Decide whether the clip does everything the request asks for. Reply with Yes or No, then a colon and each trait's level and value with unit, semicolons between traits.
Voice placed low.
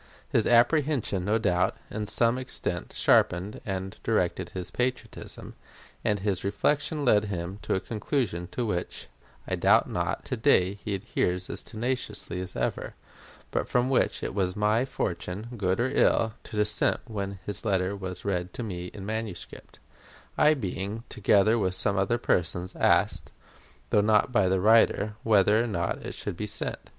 Yes: low, 105 Hz